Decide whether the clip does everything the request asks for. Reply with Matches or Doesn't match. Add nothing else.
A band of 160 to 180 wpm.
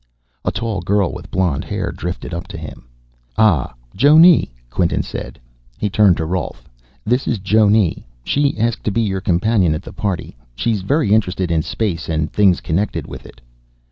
Matches